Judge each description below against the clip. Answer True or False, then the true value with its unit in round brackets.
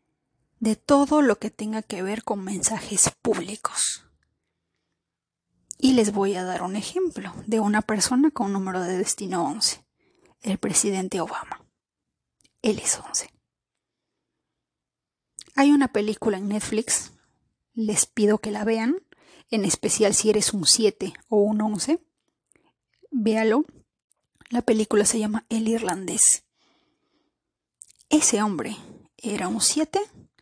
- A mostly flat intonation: False (3.8 semitones)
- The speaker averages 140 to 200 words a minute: False (125 wpm)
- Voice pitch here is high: True (220 Hz)